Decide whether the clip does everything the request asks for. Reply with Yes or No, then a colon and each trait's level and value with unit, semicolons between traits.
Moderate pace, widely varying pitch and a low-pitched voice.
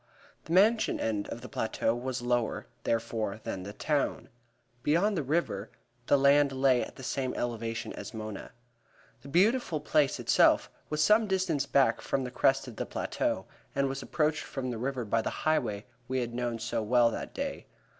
No: average, 185 wpm; average, 4.4 semitones; low, 130 Hz